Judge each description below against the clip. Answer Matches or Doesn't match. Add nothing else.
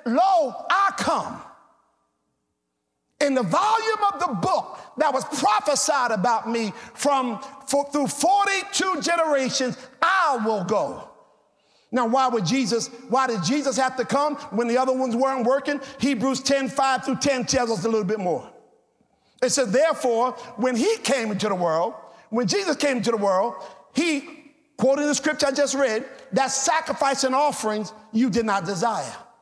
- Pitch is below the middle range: Doesn't match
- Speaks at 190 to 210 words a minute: Doesn't match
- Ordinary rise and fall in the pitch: Matches